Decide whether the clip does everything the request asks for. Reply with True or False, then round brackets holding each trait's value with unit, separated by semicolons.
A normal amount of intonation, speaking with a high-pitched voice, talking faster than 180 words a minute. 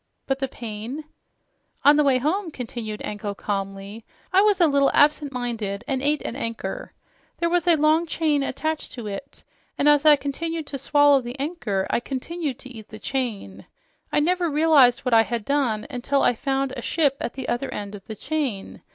True (4.9 semitones; 270 Hz; 195 wpm)